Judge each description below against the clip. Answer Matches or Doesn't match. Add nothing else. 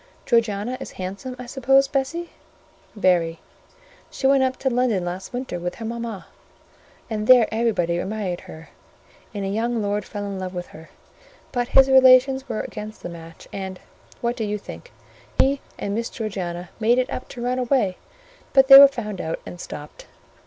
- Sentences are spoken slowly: Doesn't match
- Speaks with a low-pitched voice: Doesn't match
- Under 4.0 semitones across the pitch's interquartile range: Doesn't match